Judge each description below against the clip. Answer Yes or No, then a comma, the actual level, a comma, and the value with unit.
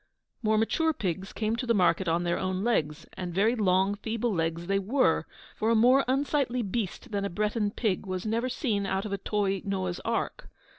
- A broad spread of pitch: No, average, 3.5 semitones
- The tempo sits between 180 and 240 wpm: Yes, average, 195 wpm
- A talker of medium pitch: No, high, 205 Hz